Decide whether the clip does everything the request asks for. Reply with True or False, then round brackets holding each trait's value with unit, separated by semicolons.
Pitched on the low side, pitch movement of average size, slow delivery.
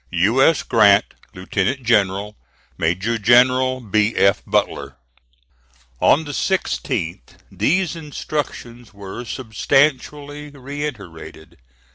False (120 Hz; 6.3 semitones; 90 wpm)